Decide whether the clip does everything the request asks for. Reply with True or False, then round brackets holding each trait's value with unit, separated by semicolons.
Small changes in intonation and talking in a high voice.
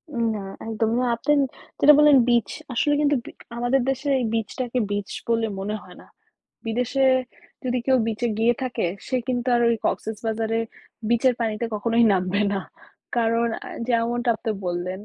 True (2.2 semitones; 235 Hz)